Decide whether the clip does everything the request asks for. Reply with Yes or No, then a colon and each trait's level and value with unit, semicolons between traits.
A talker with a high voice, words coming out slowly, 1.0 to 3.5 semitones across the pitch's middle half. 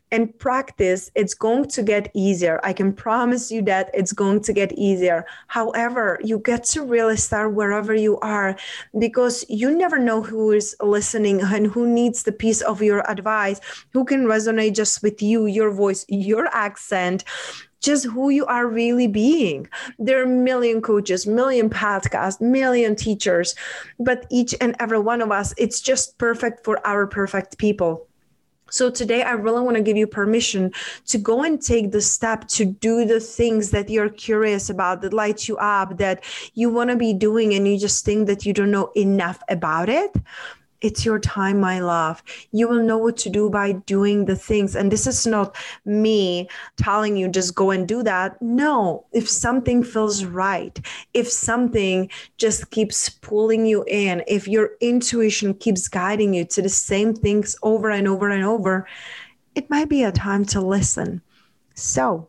No: high, 215 Hz; average, 180 wpm; average, 2.7 semitones